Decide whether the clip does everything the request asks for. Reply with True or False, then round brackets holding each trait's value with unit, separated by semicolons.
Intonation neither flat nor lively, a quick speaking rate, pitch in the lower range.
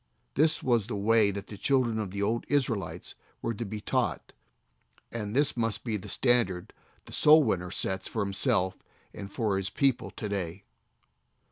False (3.5 semitones; 170 wpm; 105 Hz)